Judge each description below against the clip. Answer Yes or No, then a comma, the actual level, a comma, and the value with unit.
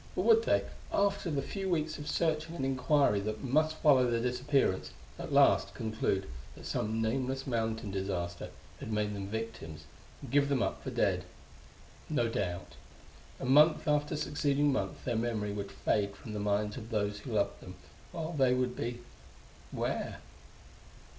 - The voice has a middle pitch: No, low, 125 Hz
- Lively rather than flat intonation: Yes, wide, 5.7 semitones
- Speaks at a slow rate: No, average, 165 wpm